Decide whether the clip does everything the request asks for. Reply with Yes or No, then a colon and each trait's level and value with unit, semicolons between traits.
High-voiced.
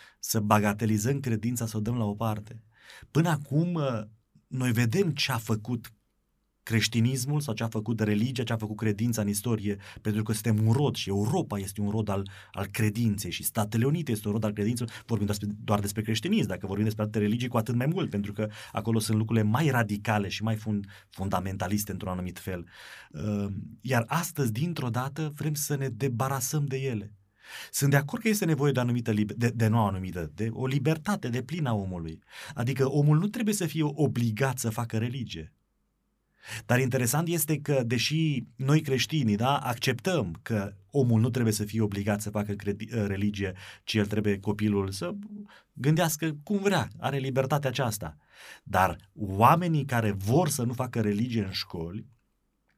No: low, 115 Hz